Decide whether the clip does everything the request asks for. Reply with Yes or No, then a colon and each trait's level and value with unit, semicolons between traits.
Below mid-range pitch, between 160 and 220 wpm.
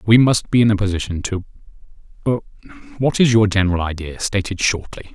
No: low, 100 Hz; average, 150 wpm